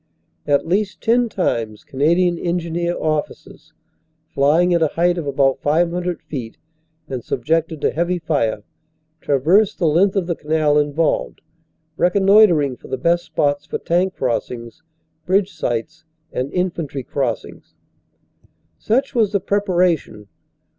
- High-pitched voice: No, medium, 165 Hz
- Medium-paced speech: No, slow, 125 wpm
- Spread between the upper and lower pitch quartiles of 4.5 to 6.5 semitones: No, average, 4.1 semitones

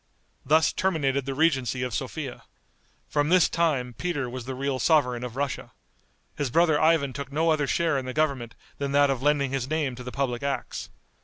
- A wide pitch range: No, average, 3.3 semitones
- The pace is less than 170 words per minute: No, average, 190 wpm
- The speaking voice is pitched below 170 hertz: Yes, medium, 140 Hz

